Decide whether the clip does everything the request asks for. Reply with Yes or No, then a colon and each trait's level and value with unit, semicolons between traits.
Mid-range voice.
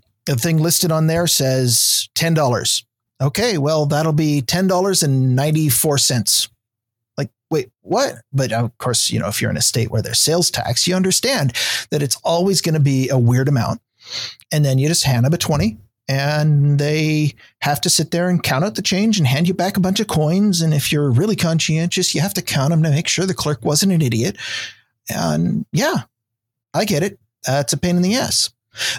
Yes: medium, 150 Hz